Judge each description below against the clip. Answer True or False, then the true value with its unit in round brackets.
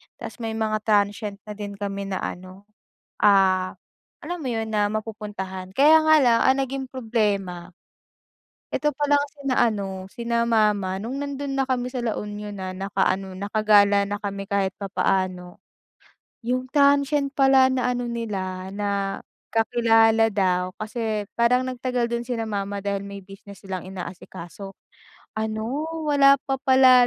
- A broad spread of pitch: False (4.1 semitones)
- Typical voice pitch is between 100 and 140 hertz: False (215 Hz)